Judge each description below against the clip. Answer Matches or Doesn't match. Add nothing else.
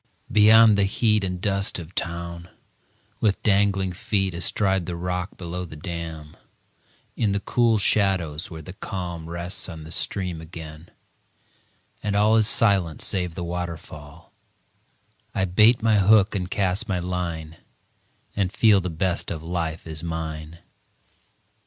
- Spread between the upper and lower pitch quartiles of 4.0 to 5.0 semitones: Doesn't match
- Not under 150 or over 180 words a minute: Doesn't match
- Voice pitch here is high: Doesn't match